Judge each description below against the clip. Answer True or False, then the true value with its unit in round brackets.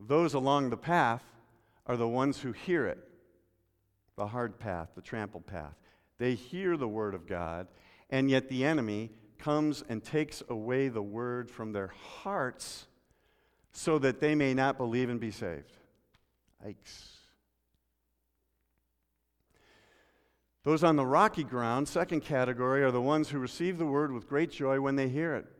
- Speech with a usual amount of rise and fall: False (5.9 semitones)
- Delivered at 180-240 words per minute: False (155 wpm)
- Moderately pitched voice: False (120 Hz)